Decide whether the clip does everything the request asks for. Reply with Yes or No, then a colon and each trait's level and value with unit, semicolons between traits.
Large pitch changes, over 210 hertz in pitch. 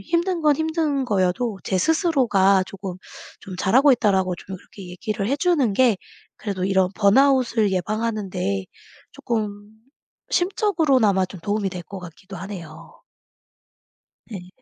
No: wide, 5.9 semitones; high, 205 Hz